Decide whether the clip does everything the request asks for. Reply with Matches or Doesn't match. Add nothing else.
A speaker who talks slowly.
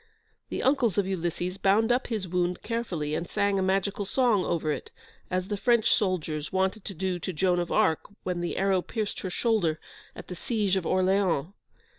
Doesn't match